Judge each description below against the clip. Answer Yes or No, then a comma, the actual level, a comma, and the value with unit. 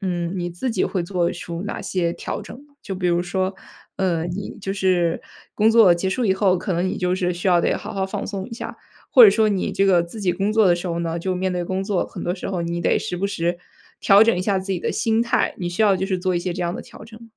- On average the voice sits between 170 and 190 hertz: Yes, medium, 185 Hz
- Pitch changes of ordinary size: No, narrow, 2.3 semitones